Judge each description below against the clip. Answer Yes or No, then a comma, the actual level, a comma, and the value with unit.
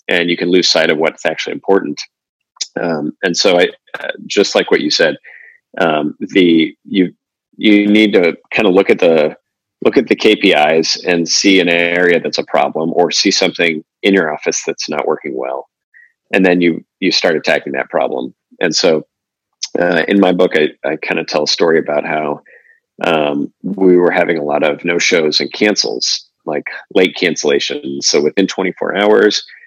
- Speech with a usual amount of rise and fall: Yes, average, 3.9 semitones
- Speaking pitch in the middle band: No, very low, 90 Hz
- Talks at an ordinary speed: Yes, average, 190 wpm